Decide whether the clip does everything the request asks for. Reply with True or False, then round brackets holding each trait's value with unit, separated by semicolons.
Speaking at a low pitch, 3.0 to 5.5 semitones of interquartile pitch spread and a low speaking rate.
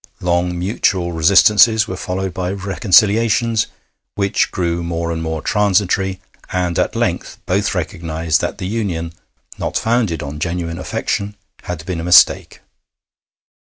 True (90 Hz; 3.3 semitones; 130 wpm)